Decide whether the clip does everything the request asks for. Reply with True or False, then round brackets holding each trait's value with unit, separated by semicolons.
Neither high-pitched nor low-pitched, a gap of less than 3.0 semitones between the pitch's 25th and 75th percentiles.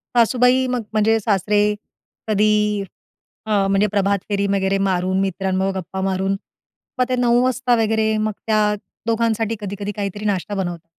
False (205 Hz; 2.5 semitones)